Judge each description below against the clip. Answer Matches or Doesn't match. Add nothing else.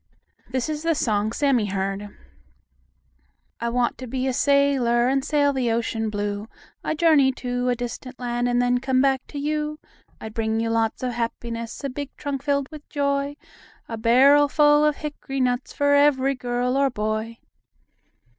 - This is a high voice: Matches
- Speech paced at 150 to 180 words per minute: Matches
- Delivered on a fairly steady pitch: Doesn't match